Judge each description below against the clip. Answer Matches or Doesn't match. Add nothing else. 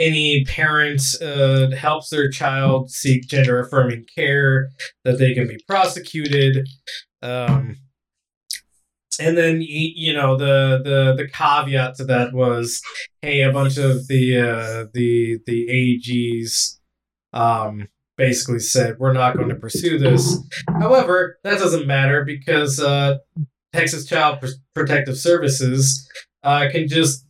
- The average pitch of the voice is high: Doesn't match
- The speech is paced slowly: Matches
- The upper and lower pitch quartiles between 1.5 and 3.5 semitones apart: Matches